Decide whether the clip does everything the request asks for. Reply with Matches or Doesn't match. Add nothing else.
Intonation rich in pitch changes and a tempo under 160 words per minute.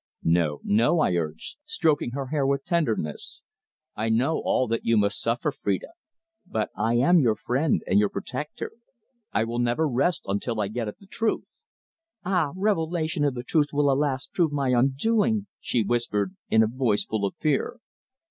Doesn't match